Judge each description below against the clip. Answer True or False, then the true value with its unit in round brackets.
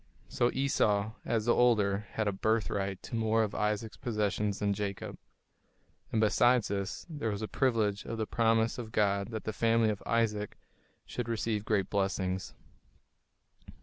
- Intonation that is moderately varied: False (2.1 semitones)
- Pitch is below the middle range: True (110 Hz)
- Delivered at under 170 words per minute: True (155 wpm)